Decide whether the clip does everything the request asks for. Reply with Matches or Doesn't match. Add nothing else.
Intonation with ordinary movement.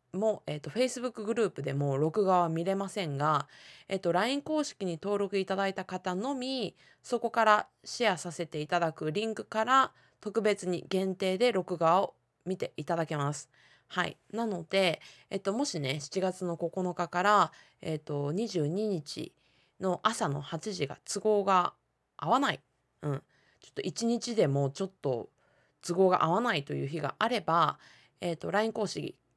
Matches